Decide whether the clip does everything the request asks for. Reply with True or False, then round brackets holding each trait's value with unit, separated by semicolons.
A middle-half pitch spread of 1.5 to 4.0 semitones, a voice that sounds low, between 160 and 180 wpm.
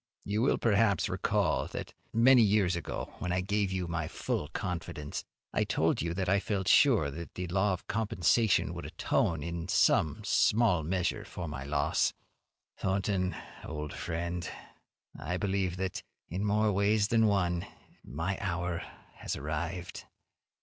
False (3.2 semitones; 90 Hz; 145 wpm)